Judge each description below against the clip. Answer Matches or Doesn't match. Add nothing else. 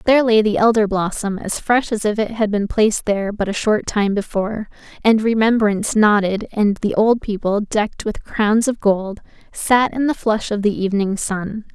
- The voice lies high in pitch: Matches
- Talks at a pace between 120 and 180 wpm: Doesn't match